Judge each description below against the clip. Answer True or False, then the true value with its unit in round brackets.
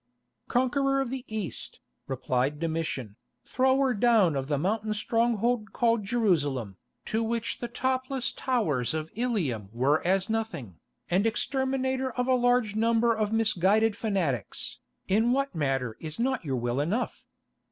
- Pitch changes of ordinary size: False (8.0 semitones)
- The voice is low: False (220 Hz)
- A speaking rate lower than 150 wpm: True (140 wpm)